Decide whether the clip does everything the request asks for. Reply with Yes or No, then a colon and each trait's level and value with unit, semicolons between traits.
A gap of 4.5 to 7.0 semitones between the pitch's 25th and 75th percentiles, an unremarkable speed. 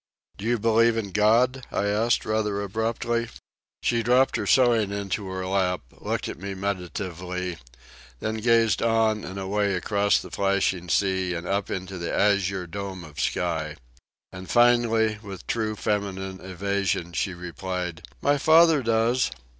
No: average, 3.3 semitones; average, 145 wpm